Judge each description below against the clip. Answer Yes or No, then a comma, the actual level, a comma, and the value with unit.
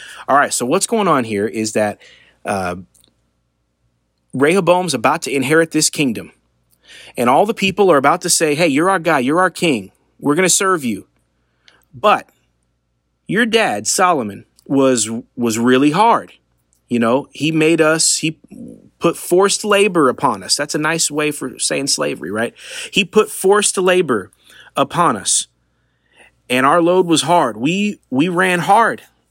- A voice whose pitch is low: No, medium, 150 Hz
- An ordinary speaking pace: Yes, average, 160 wpm